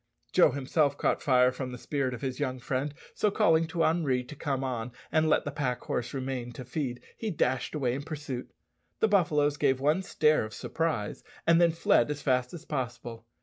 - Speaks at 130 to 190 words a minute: No, average, 200 wpm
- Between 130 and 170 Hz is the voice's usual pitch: Yes, medium, 140 Hz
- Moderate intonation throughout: Yes, average, 3.6 semitones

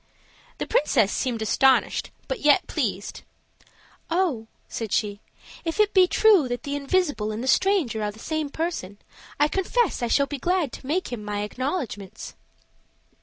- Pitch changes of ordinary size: No, wide, 7.9 semitones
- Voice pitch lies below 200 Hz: No, very high, 275 Hz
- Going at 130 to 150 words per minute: No, average, 160 wpm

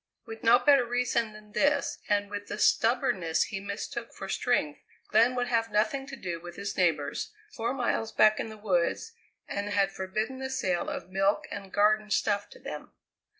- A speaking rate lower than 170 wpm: No, average, 185 wpm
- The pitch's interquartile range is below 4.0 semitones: Yes, average, 3.5 semitones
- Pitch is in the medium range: No, high, 215 Hz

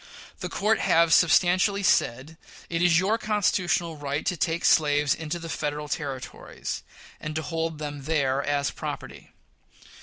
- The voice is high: No, medium, 160 Hz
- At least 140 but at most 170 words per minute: Yes, average, 145 wpm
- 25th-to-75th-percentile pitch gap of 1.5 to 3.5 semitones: Yes, average, 3.2 semitones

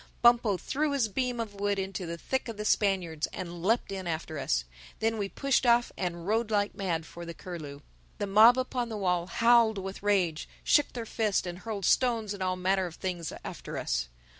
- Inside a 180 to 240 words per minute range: Yes, fast, 205 wpm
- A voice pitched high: Yes, high, 195 Hz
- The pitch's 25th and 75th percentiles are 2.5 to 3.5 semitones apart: No, average, 4.4 semitones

